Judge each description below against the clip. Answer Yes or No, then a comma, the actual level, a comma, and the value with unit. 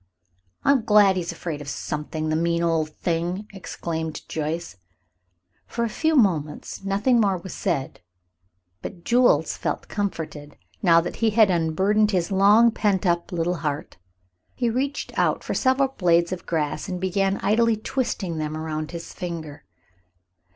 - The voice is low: No, medium, 180 Hz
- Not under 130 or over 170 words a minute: Yes, average, 150 wpm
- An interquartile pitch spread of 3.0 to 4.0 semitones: No, average, 4.6 semitones